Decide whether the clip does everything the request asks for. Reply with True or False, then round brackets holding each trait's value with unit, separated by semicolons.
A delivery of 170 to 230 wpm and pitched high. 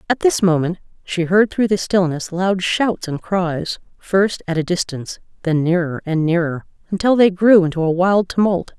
False (185 wpm; 180 Hz)